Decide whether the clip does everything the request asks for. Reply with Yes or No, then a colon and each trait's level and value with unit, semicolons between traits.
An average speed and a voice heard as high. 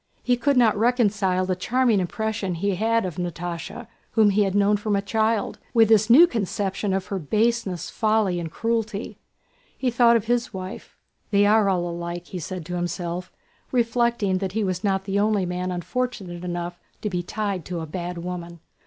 Yes: average, 185 wpm; high, 200 Hz